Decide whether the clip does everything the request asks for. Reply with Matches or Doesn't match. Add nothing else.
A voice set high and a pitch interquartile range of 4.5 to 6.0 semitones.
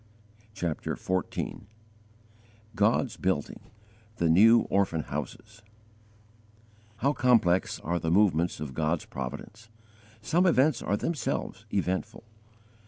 Doesn't match